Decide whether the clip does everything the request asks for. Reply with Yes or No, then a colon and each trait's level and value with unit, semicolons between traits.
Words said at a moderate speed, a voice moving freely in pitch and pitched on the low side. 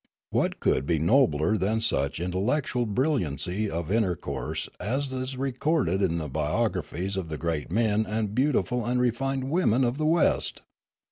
Yes: average, 155 wpm; wide, 7.1 semitones; low, 110 Hz